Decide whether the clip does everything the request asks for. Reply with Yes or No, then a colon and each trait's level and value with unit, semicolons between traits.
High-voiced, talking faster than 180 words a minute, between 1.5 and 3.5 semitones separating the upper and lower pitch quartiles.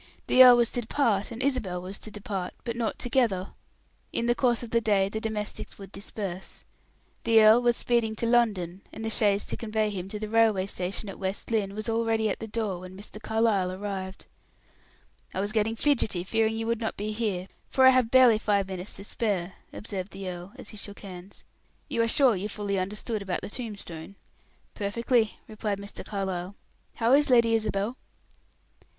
Yes: high, 215 Hz; average, 195 wpm; average, 2.8 semitones